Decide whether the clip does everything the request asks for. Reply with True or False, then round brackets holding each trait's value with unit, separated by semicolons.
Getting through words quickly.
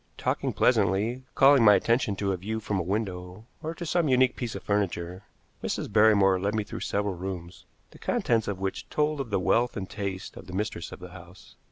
True (210 wpm)